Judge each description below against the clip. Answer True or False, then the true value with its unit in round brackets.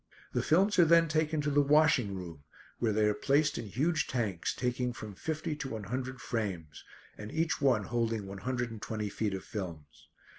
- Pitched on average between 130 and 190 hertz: False (120 Hz)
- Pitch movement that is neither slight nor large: False (6.3 semitones)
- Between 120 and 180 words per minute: False (195 wpm)